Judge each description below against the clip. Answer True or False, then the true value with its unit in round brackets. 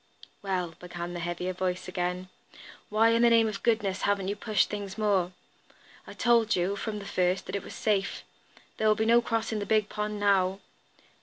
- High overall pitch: True (200 Hz)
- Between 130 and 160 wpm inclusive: False (190 wpm)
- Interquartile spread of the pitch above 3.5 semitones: False (2.8 semitones)